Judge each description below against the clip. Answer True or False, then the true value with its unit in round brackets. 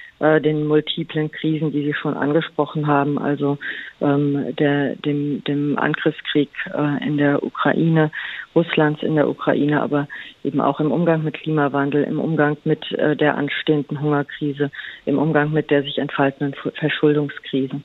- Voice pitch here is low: False (145 Hz)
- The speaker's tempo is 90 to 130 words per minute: False (140 wpm)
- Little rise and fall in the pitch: True (1.2 semitones)